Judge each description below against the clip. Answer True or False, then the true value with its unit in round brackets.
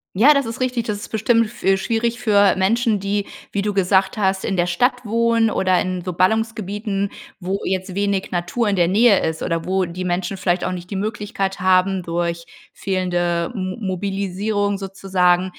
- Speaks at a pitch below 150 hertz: False (195 Hz)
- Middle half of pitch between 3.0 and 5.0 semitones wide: False (2.6 semitones)